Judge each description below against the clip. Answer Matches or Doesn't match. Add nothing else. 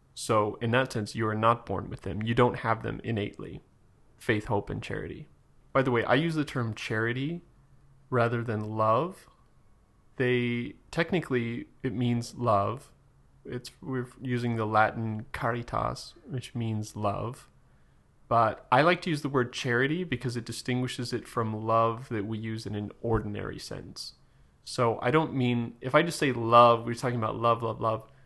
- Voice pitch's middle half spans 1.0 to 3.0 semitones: Matches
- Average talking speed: Matches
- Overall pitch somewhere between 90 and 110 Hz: Doesn't match